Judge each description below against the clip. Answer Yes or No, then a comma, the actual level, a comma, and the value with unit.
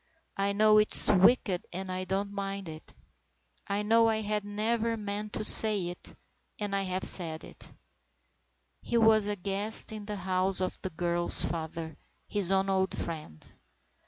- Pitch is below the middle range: No, high, 195 Hz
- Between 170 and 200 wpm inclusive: No, average, 160 wpm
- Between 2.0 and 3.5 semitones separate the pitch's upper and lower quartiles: Yes, narrow, 2.4 semitones